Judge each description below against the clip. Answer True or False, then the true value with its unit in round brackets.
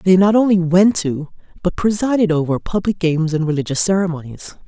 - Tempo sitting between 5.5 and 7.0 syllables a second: True (5.7 syllables/s)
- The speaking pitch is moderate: True (180 Hz)